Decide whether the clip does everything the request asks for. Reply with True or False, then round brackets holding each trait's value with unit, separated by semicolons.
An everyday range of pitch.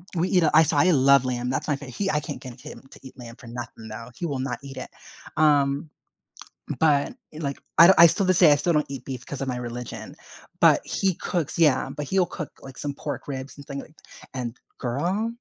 True (3.7 semitones)